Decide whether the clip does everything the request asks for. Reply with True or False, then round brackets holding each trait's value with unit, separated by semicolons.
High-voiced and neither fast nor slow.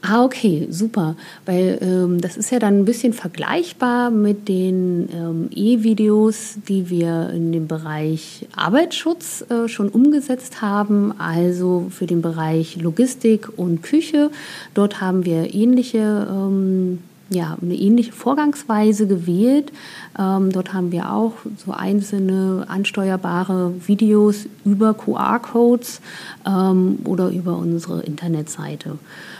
False (195 Hz; 120 wpm)